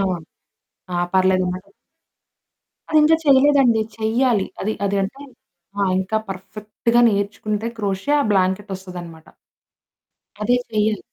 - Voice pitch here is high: Yes, high, 205 Hz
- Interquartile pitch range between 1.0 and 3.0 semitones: No, average, 3.6 semitones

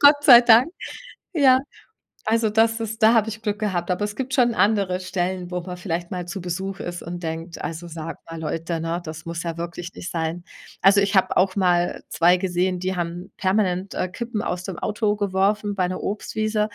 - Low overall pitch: No, medium, 185 Hz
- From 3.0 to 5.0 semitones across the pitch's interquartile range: Yes, average, 3.4 semitones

